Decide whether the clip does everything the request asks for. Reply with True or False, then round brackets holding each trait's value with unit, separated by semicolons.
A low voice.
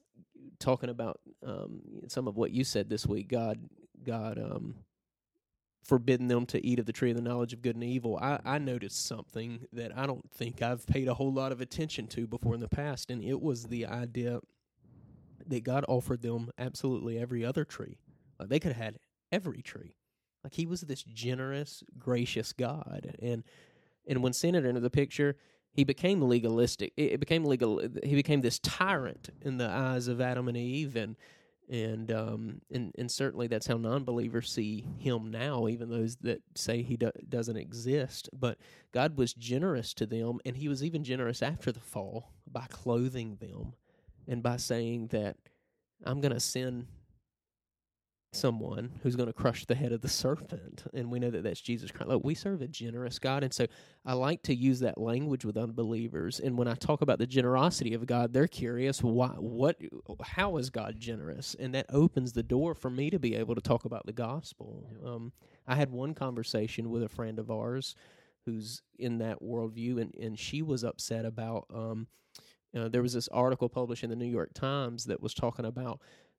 True (120 Hz)